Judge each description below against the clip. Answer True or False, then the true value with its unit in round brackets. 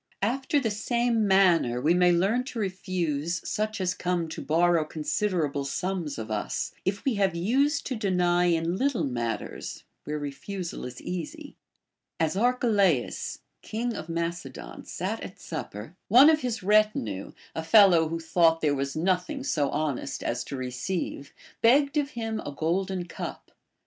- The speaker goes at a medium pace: True (160 wpm)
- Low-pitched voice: False (180 Hz)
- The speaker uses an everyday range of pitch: False (5.7 semitones)